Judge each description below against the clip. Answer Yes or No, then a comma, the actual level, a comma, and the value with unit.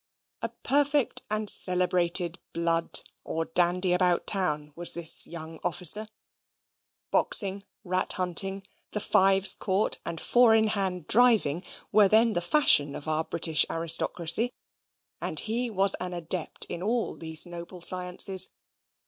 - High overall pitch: No, medium, 180 Hz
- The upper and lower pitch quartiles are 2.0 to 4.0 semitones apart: Yes, average, 3.4 semitones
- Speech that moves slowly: Yes, slow, 130 wpm